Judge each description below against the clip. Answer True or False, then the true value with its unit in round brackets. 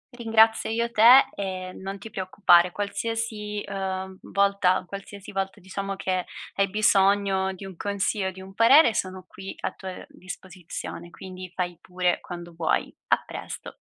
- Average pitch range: False (1.8 semitones)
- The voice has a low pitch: False (195 Hz)